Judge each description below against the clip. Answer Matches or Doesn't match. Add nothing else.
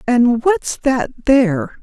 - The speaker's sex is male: Doesn't match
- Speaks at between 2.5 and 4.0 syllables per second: Matches